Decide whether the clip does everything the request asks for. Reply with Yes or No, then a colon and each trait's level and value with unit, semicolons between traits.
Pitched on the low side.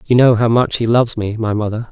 Yes: low, 115 Hz